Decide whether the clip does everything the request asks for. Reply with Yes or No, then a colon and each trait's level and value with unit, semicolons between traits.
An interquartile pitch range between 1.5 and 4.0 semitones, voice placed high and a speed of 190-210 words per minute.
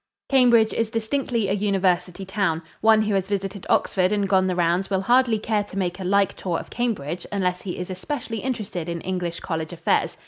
Yes: average, 3.3 semitones; high, 195 Hz; average, 200 wpm